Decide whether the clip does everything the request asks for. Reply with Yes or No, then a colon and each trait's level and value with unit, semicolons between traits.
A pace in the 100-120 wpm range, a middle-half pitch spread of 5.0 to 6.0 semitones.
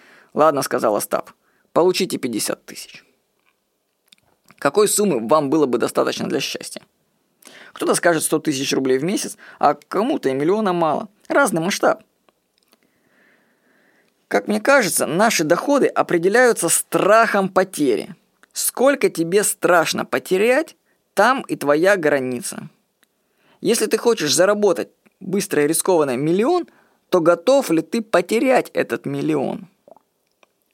Yes: average, 115 wpm; wide, 5.5 semitones